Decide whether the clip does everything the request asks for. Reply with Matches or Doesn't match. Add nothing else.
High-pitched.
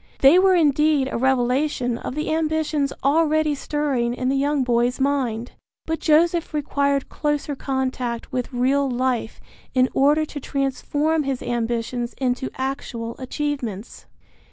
Matches